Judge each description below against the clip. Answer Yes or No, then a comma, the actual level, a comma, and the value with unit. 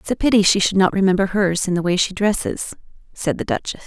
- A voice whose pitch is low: No, high, 190 Hz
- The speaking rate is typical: No, fast, 250 wpm